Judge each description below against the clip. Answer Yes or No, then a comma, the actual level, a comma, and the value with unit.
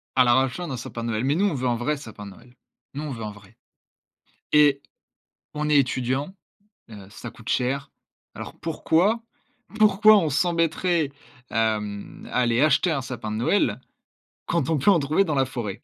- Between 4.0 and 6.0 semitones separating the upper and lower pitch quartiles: Yes, average, 5.2 semitones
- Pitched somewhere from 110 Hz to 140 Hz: Yes, low, 135 Hz